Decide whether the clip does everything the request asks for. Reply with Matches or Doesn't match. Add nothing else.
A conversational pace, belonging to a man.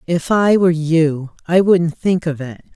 Doesn't match